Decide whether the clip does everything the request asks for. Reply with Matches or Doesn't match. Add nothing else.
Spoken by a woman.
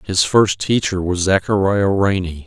Doesn't match